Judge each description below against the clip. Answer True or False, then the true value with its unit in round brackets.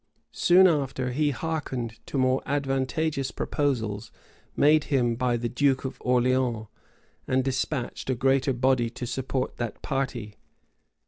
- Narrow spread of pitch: True (2.2 semitones)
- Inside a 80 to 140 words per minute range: True (135 wpm)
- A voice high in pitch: False (130 Hz)